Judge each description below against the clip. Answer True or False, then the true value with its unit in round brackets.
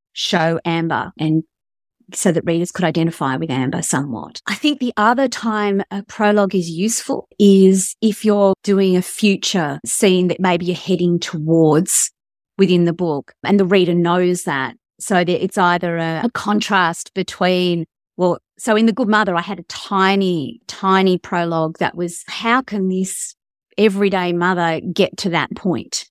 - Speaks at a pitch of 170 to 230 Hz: True (185 Hz)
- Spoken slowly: False (165 wpm)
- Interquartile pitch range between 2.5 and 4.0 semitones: True (2.9 semitones)